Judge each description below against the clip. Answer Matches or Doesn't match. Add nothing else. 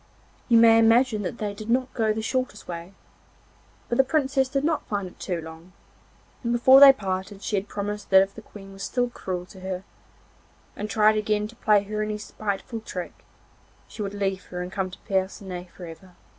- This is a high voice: Matches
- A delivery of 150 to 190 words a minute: Doesn't match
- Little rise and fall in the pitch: Doesn't match